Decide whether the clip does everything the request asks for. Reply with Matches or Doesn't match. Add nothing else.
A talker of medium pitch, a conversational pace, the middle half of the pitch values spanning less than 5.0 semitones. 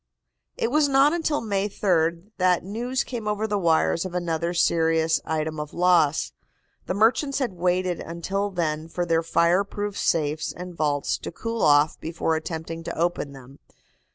Matches